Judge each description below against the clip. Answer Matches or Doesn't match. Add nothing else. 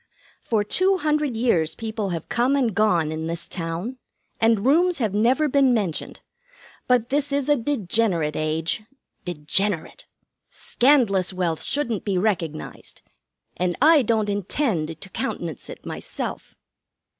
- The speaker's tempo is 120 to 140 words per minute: Matches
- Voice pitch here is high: Matches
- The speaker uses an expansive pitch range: Matches